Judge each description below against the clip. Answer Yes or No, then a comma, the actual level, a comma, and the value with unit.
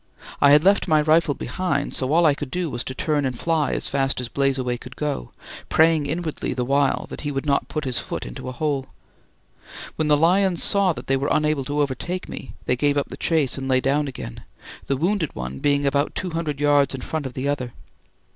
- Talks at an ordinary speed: No, fast, 225 wpm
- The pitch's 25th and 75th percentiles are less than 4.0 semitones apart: Yes, average, 2.7 semitones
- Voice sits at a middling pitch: Yes, medium, 145 Hz